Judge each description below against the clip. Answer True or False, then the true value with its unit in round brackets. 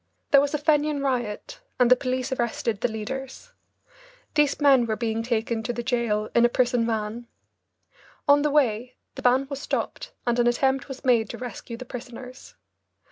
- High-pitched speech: True (245 Hz)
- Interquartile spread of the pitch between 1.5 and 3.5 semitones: True (2.6 semitones)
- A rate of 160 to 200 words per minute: True (180 wpm)